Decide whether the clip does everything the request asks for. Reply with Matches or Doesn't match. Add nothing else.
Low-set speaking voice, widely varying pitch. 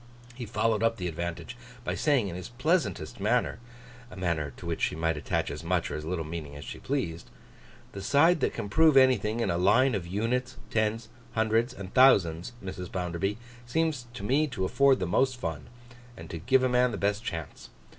Matches